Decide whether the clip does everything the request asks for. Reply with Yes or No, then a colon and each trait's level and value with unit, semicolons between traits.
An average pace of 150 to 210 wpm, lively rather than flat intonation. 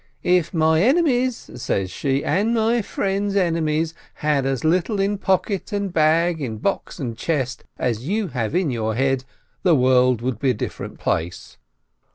Yes: average, 170 wpm; wide, 7.2 semitones